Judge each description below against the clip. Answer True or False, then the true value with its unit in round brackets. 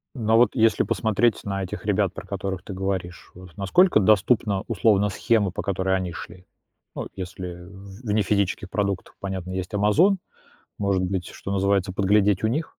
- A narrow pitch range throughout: True (2.2 semitones)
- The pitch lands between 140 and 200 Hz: False (100 Hz)